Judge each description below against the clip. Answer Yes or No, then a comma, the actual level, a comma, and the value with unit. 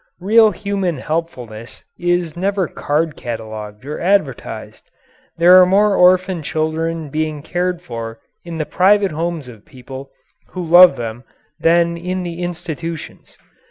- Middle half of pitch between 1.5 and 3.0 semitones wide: No, average, 4.2 semitones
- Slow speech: Yes, slow, 130 wpm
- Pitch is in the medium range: Yes, medium, 165 Hz